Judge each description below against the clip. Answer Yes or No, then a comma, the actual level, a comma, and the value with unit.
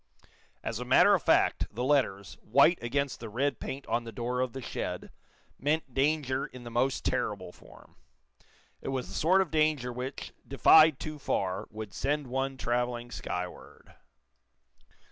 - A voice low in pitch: Yes, low, 130 Hz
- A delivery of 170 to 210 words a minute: No, average, 160 wpm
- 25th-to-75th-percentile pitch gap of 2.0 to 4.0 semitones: Yes, average, 3.1 semitones